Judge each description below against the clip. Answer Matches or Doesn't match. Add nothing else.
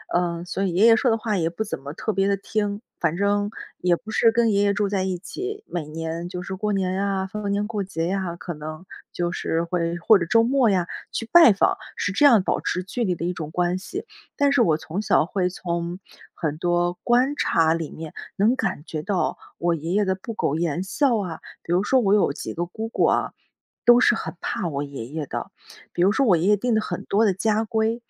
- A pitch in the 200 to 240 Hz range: Doesn't match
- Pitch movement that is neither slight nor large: Matches